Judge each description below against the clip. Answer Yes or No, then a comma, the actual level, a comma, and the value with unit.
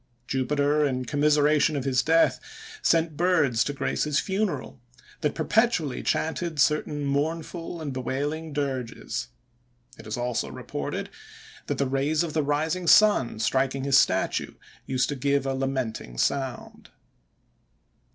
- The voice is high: No, medium, 145 Hz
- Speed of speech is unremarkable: No, slow, 130 wpm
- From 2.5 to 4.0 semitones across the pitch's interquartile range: Yes, average, 3.1 semitones